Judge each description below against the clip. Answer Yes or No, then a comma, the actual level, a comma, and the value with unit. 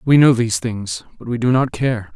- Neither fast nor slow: No, fast, 250 wpm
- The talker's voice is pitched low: Yes, low, 120 Hz